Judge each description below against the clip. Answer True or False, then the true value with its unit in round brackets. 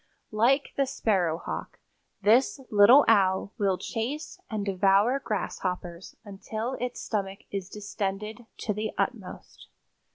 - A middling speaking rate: False (110 wpm)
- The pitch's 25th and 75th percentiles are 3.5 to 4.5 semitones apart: False (3.1 semitones)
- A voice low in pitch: False (210 Hz)